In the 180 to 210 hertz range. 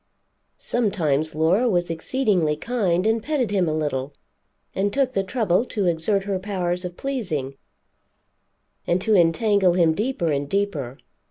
Yes: medium, 185 Hz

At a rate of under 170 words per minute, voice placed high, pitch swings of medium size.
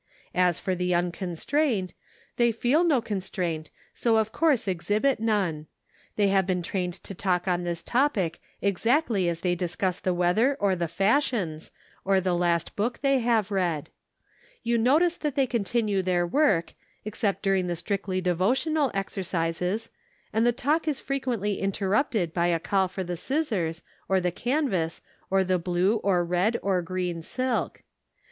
Yes: average, 160 wpm; high, 195 Hz; average, 4.9 semitones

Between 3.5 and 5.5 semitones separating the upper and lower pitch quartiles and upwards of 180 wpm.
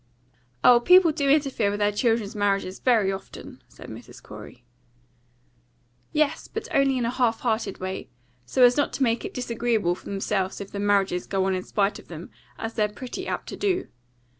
Yes: average, 4.3 semitones; average, 190 wpm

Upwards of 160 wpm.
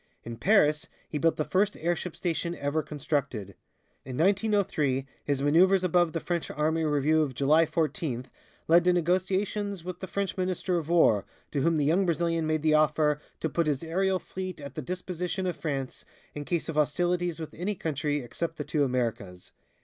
Yes: average, 180 wpm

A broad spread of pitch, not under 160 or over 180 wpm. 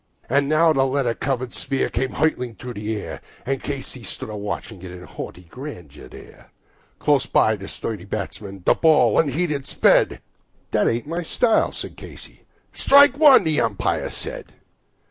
Yes: wide, 6.3 semitones; average, 165 wpm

